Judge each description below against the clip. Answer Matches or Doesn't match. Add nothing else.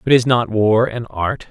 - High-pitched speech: Doesn't match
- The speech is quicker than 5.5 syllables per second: Doesn't match